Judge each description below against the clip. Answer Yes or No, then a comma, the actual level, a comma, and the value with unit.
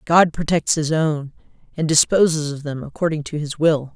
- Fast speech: No, average, 180 wpm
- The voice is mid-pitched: Yes, medium, 155 Hz